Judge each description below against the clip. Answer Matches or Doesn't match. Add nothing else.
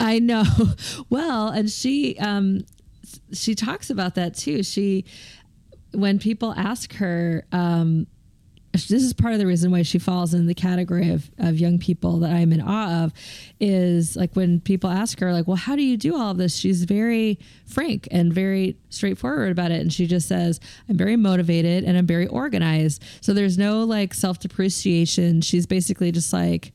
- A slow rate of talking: Doesn't match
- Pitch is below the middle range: Doesn't match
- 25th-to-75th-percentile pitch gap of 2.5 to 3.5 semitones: Matches